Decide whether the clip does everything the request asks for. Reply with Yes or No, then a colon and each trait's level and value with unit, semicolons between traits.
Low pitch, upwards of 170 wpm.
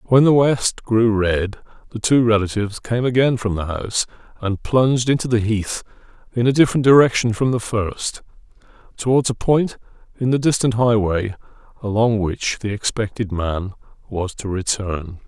No: low, 110 Hz; average, 155 wpm